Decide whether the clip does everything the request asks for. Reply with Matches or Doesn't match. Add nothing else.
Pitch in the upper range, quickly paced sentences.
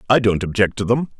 Doesn't match